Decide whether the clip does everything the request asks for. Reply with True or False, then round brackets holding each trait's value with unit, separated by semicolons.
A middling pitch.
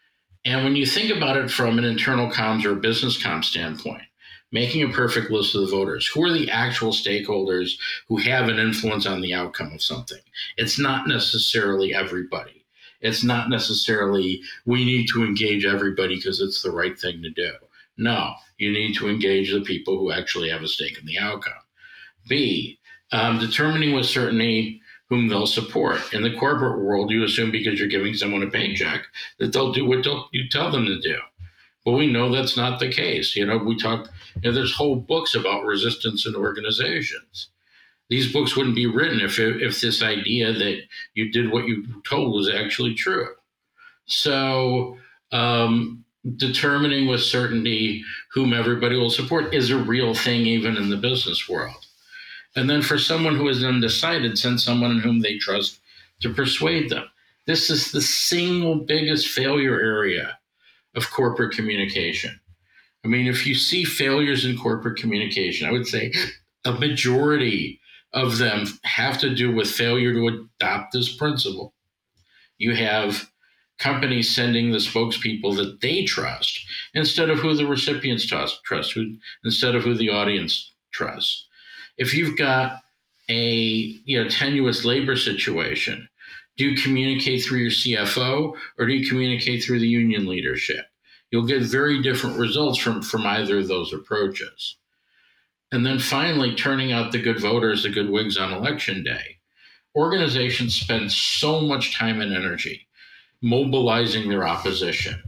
False (120 Hz)